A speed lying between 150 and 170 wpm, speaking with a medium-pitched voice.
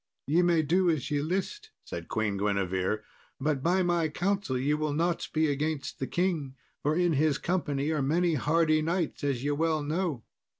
No: average, 180 wpm; medium, 155 Hz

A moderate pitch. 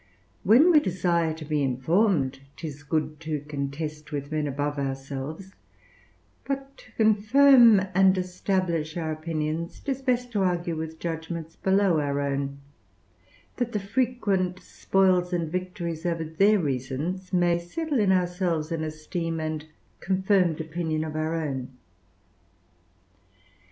Yes: medium, 170 Hz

